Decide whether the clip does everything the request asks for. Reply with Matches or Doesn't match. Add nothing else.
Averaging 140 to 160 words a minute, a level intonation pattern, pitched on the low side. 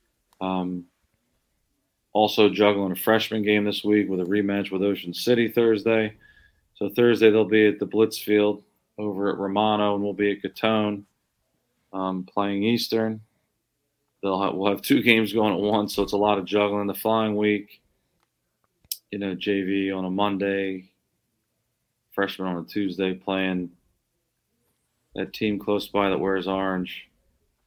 Matches